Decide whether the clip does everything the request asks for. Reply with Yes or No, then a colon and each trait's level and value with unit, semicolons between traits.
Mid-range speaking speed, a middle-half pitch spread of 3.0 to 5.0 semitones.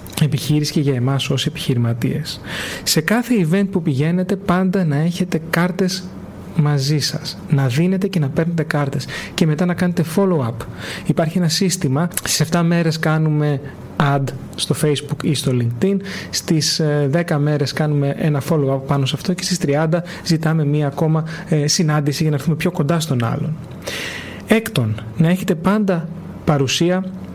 Yes: average, 150 wpm; average, 3.6 semitones